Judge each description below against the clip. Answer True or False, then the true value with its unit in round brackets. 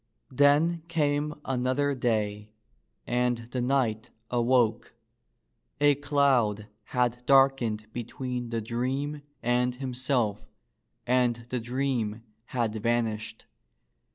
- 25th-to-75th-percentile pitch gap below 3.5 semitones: True (2.7 semitones)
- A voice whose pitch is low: True (125 Hz)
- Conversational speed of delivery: False (95 wpm)